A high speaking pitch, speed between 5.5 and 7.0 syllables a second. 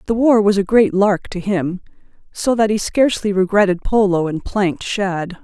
No: high, 200 Hz; 5.0 syllables/s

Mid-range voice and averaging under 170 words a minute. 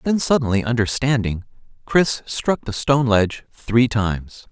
No: low, 120 Hz; slow, 135 wpm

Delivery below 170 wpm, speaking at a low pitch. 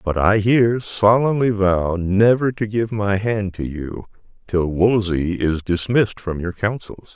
Yes: average, 160 wpm; low, 100 Hz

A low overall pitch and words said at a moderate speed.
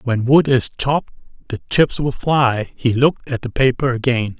Yes: low, 130 Hz; average, 190 wpm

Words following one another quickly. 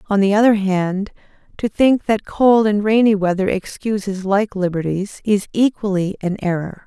No: average, 155 wpm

